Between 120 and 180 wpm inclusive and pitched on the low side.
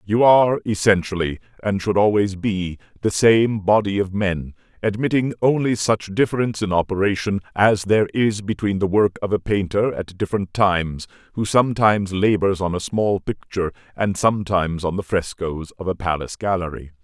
Yes: average, 160 wpm; low, 100 Hz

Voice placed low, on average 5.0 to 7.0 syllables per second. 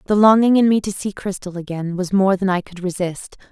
No: high, 190 Hz; 5.6 syllables/s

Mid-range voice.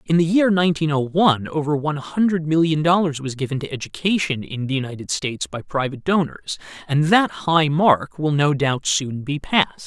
Yes: medium, 150 Hz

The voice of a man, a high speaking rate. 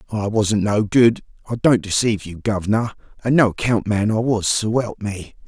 No: male; average, 165 wpm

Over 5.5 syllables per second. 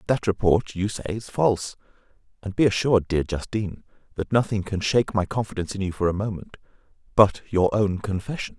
Yes: 5.9 syllables/s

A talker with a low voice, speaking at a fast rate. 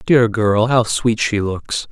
No: low, 110 Hz; average, 190 wpm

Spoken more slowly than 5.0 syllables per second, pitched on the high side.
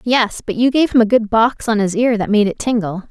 No: 5.5 syllables/s; high, 220 Hz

